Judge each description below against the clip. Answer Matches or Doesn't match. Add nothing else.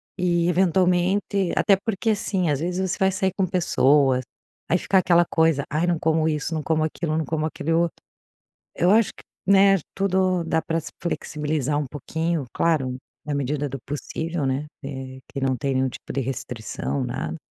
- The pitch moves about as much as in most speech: Matches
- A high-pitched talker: Doesn't match